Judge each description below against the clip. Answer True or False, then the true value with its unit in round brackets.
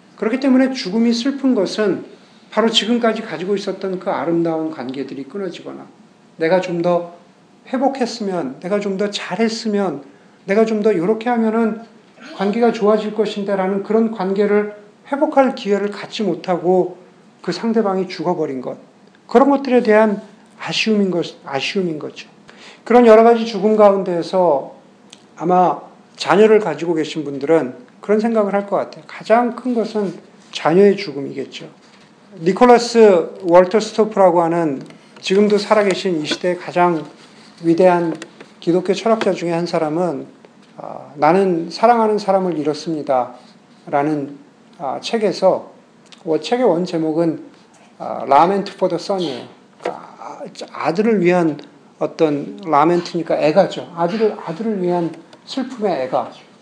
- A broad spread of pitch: False (4.5 semitones)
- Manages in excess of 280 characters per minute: True (290 characters per minute)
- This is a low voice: False (200 Hz)